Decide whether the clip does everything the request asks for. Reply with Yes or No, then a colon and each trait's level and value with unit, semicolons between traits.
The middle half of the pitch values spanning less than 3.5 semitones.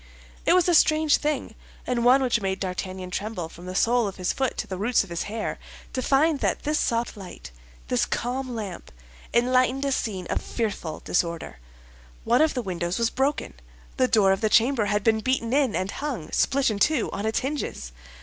No: wide, 5.5 semitones